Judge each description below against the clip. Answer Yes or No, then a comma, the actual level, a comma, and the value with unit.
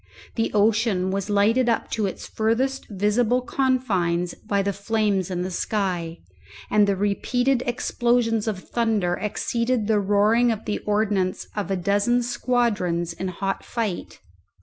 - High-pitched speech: Yes, high, 210 Hz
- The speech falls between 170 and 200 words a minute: No, average, 145 wpm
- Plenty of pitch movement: No, average, 3.3 semitones